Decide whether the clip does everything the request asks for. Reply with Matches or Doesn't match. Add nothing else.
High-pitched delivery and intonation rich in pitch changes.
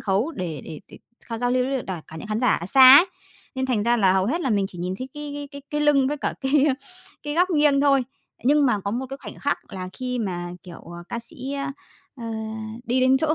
Matches